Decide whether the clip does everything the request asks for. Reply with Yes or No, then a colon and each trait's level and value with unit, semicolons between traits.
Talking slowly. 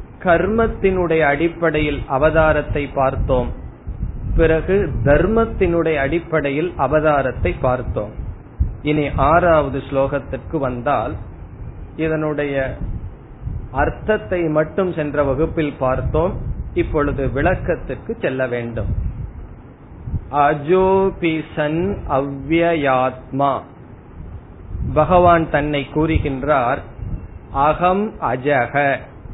Yes: slow, 60 wpm